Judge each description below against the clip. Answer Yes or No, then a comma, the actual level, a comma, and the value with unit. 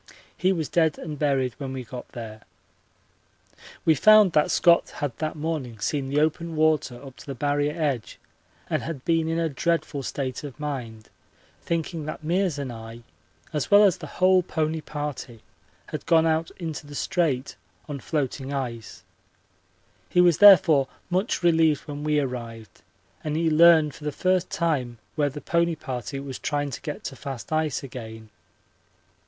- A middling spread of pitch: Yes, average, 3.5 semitones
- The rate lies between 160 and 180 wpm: Yes, average, 170 wpm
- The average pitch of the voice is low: No, medium, 150 Hz